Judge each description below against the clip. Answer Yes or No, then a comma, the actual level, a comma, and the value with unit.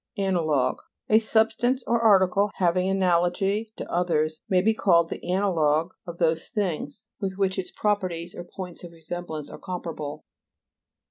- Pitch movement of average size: Yes, average, 3.0 semitones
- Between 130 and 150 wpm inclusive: Yes, average, 145 wpm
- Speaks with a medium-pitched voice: Yes, medium, 180 Hz